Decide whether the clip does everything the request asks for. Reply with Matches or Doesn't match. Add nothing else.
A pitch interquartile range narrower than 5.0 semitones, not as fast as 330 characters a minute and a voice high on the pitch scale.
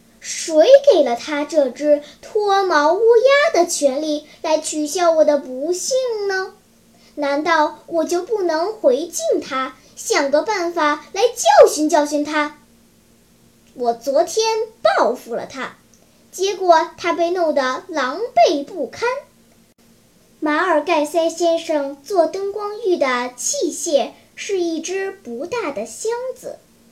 Matches